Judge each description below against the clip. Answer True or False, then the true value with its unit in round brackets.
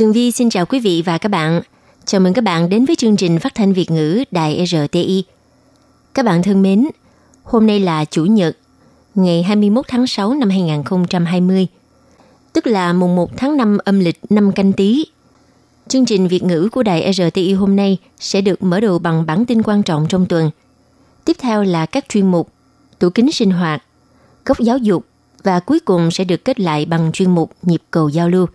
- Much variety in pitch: False (4.3 semitones)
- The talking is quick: False (200 wpm)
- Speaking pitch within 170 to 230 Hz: True (190 Hz)